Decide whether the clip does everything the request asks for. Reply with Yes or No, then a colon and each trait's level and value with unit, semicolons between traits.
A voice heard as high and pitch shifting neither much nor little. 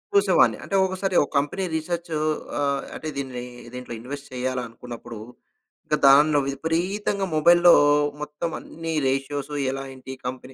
No: medium, 145 Hz; average, 4.4 semitones